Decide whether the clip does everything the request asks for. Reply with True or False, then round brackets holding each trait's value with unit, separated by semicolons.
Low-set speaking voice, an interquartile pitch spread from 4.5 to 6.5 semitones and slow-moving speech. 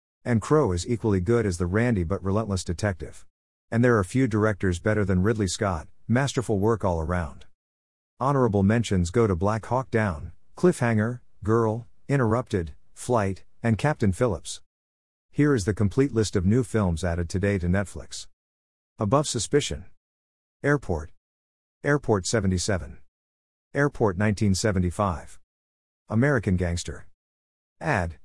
True (100 Hz; 5.5 semitones; 125 wpm)